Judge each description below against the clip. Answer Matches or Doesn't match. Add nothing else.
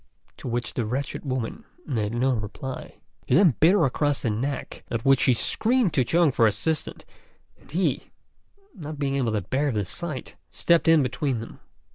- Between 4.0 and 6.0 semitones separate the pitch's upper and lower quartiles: Matches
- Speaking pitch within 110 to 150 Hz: Matches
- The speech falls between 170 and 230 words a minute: Matches